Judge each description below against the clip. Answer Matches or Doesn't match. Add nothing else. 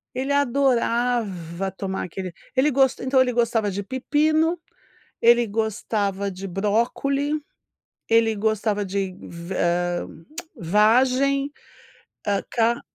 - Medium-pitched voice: Doesn't match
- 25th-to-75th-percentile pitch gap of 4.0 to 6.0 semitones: Matches